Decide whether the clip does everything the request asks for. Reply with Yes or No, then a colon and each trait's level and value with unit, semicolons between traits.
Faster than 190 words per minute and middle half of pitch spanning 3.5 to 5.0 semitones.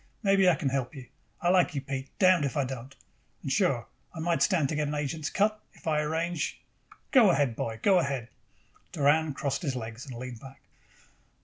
Yes: average, 200 wpm; average, 4.4 semitones